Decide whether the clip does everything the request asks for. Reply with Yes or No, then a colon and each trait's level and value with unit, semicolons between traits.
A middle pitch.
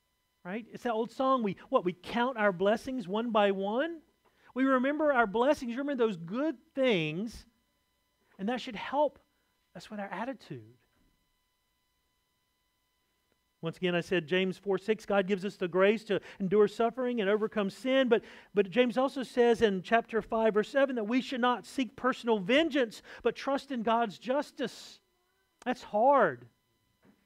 No: high, 225 Hz